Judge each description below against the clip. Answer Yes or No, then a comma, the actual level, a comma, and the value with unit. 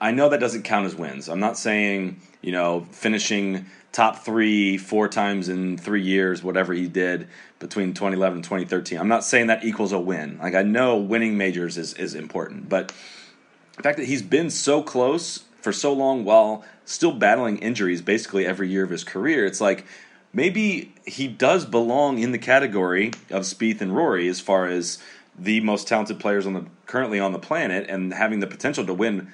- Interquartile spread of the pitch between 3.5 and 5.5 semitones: No, average, 3.1 semitones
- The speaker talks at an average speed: Yes, average, 195 wpm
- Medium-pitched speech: No, low, 100 Hz